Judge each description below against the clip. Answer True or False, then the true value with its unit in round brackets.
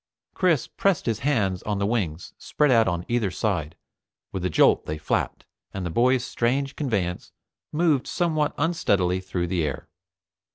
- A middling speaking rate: True (160 wpm)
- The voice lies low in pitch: True (105 Hz)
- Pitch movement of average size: False (7.6 semitones)